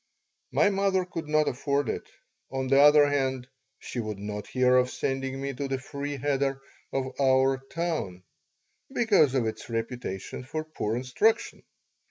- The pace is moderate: Yes, average, 155 wpm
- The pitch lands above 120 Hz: Yes, low, 135 Hz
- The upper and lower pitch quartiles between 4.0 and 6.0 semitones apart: No, narrow, 2.6 semitones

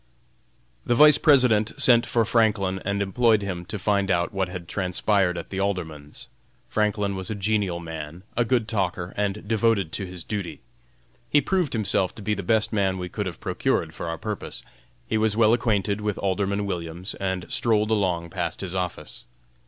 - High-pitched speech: No, low, 100 Hz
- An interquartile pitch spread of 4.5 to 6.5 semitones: No, average, 3.0 semitones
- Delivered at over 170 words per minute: Yes, average, 180 wpm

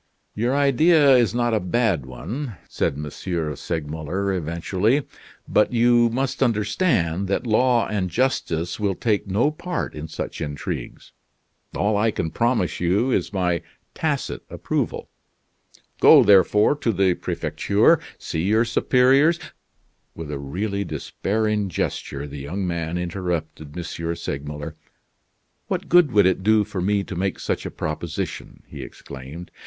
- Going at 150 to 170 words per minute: No, average, 140 wpm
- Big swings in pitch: Yes, wide, 6.1 semitones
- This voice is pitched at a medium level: No, low, 100 Hz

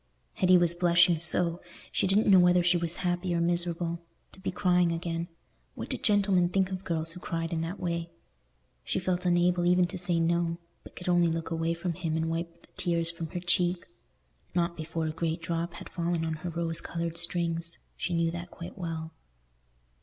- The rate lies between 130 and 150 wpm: No, average, 190 wpm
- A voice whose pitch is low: No, medium, 170 Hz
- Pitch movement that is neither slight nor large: No, narrow, 1.2 semitones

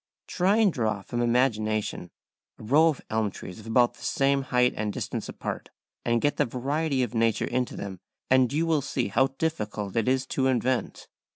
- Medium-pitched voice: No, low, 125 Hz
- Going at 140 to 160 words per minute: No, average, 190 wpm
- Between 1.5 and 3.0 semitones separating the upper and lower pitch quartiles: No, average, 3.8 semitones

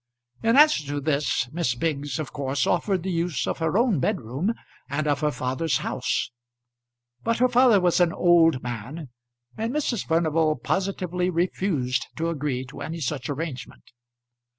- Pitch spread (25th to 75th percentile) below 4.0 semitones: No, average, 4.6 semitones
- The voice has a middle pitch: Yes, medium, 160 Hz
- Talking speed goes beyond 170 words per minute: No, average, 155 wpm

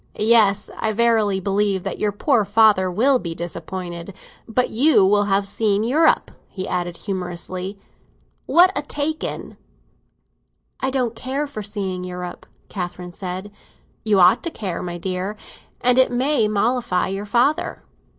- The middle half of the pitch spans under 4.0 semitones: No, average, 4.5 semitones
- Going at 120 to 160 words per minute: Yes, average, 145 wpm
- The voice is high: Yes, high, 205 Hz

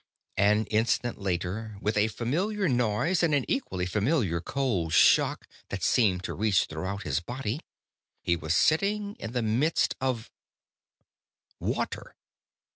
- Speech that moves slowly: Yes, slow, 130 wpm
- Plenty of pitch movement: Yes, wide, 6.6 semitones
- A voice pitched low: Yes, low, 110 Hz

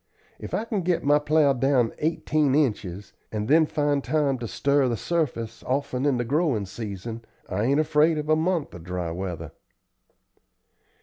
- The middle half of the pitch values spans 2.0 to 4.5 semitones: No, wide, 5.4 semitones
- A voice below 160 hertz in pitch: Yes, medium, 140 Hz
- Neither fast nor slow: Yes, average, 170 wpm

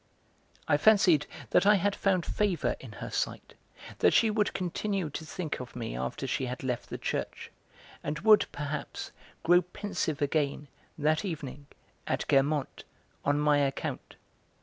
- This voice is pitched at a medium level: Yes, medium, 150 Hz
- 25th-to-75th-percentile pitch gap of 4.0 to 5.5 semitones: Yes, average, 5.1 semitones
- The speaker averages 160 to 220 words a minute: No, average, 150 wpm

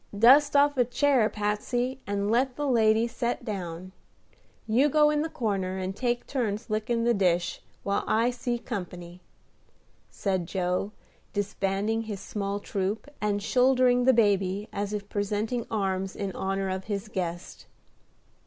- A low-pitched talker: No, high, 210 Hz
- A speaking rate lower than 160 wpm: Yes, average, 145 wpm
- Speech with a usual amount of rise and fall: Yes, average, 3.9 semitones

